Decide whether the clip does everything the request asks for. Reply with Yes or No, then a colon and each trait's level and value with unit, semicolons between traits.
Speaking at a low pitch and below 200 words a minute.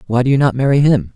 No: low, 125 Hz; fast, 315 wpm